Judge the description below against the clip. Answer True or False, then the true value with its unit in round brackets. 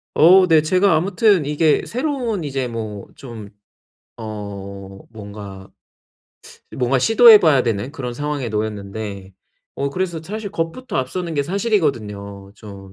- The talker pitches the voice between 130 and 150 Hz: True (135 Hz)